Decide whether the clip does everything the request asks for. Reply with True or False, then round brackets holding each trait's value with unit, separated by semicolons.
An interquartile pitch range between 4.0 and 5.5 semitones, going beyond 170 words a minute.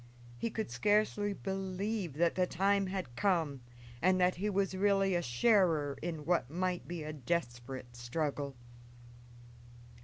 False (5.0 semitones; 140 wpm)